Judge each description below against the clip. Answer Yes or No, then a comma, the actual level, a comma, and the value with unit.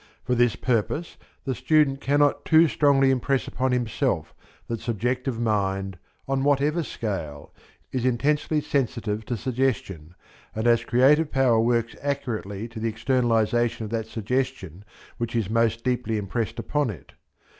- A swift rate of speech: No, average, 140 wpm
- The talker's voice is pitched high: No, low, 120 Hz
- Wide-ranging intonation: No, average, 3.4 semitones